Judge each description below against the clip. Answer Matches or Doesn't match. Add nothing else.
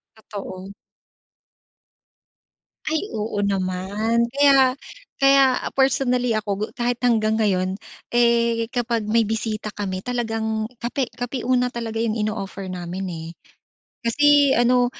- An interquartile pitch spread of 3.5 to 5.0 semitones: Doesn't match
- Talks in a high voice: Matches